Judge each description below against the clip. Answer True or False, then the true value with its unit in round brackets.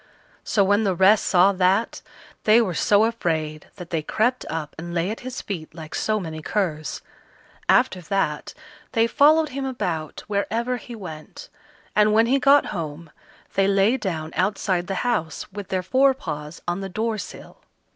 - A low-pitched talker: False (195 Hz)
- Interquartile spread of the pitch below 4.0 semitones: False (5.2 semitones)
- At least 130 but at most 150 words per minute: False (170 wpm)